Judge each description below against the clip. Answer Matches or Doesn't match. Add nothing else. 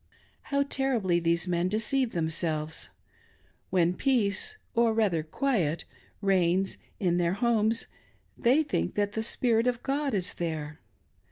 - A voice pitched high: Matches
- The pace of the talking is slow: Matches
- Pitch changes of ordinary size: Doesn't match